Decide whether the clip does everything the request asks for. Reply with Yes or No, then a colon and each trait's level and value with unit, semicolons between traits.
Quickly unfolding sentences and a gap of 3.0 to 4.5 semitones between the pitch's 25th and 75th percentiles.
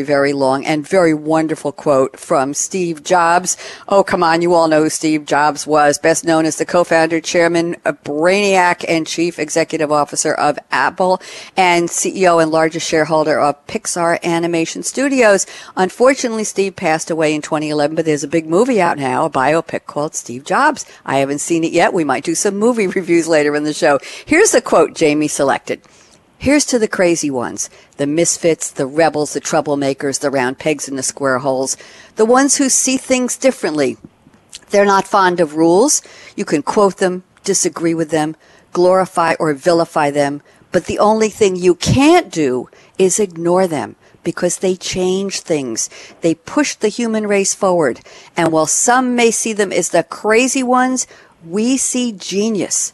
No: average, 175 wpm; average, 4.2 semitones